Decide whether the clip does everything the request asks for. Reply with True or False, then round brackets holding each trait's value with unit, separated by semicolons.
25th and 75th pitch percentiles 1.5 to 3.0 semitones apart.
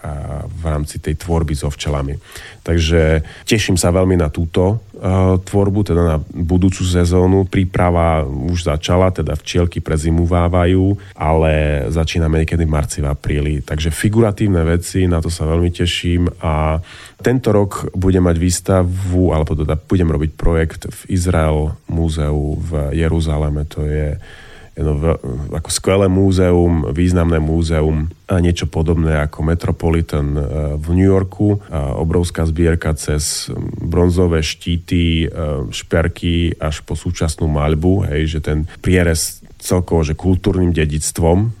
True (2.7 semitones)